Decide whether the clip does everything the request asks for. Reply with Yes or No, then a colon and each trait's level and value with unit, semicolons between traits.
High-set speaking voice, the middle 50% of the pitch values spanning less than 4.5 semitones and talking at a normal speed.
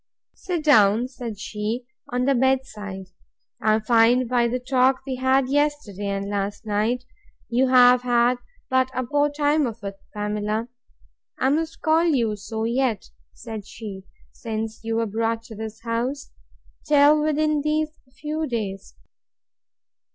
Yes: high, 240 Hz; average, 3.9 semitones; average, 145 wpm